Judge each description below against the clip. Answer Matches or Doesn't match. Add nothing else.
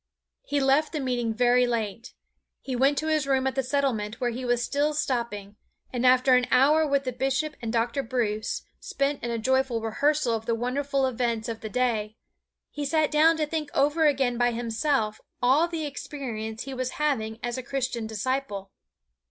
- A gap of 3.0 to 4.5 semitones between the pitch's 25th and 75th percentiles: Matches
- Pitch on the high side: Matches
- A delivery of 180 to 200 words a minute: Matches